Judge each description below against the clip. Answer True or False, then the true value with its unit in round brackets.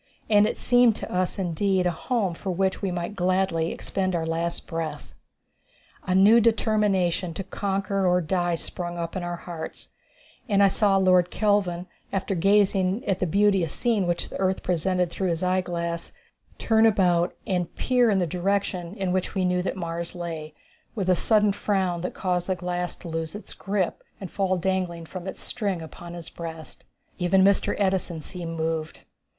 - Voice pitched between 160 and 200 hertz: True (185 Hz)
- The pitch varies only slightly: True (2.3 semitones)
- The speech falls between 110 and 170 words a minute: False (180 wpm)